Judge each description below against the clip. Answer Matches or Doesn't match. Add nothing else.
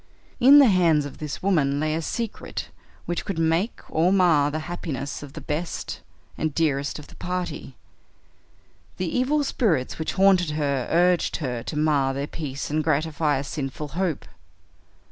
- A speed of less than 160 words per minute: Doesn't match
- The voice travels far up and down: Doesn't match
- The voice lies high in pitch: Doesn't match